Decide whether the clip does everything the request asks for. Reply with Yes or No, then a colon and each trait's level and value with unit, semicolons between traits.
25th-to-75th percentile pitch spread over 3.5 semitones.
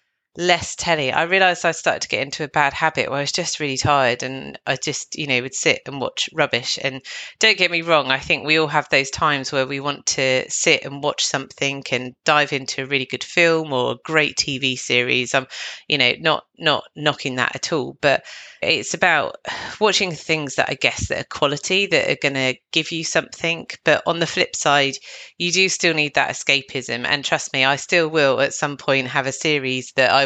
No: average, 3.2 semitones